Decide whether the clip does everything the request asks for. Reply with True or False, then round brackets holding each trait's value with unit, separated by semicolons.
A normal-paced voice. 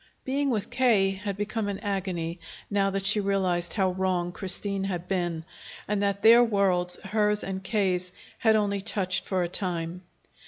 True (165 wpm)